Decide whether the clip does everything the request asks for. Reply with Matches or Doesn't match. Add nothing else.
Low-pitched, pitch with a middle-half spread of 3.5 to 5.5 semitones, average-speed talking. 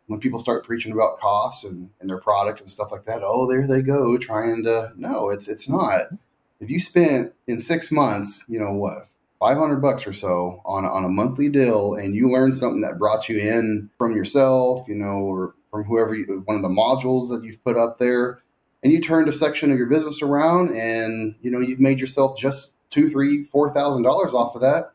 Doesn't match